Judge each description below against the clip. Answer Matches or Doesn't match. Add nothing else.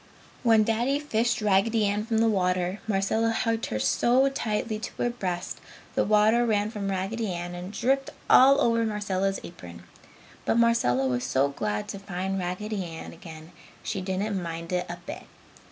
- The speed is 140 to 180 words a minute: Matches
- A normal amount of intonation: Matches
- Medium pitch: Doesn't match